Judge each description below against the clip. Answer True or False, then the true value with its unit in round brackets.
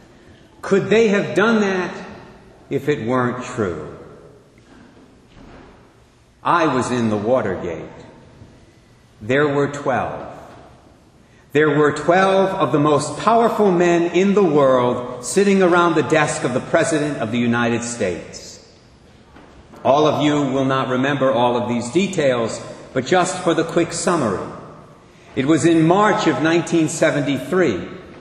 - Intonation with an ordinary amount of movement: False (5.7 semitones)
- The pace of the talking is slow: True (130 wpm)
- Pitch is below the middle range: False (150 Hz)